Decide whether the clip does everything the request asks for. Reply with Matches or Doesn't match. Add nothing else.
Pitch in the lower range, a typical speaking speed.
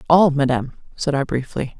Doesn't match